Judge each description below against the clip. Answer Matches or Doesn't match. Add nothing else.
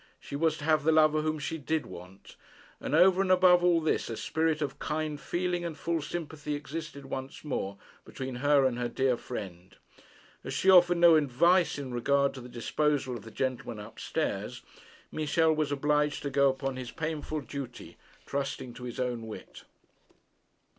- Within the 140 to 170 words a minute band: Doesn't match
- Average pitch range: Matches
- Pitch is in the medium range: Matches